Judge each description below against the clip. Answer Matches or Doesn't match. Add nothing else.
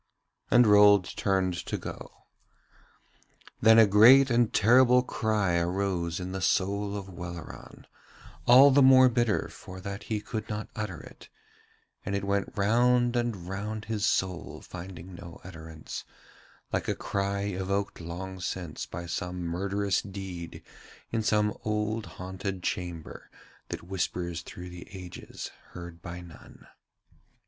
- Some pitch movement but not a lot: Matches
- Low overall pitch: Matches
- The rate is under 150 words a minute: Matches